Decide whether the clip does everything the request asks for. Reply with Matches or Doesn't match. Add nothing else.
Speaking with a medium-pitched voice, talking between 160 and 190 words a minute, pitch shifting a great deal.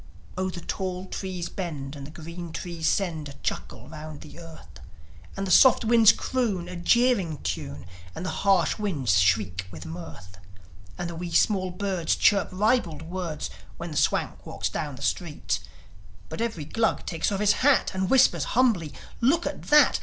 Doesn't match